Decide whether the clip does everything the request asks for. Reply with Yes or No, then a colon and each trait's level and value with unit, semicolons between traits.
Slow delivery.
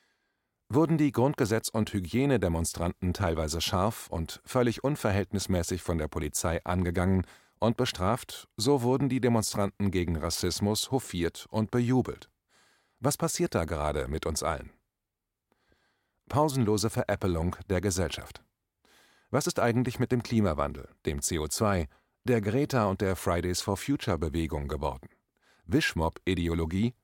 Yes: slow, 120 wpm